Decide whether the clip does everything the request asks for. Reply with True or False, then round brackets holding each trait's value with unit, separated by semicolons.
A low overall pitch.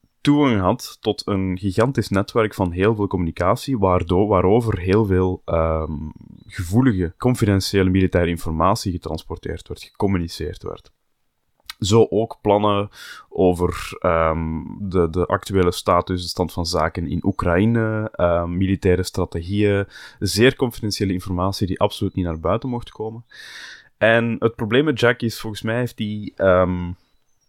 True (95 Hz)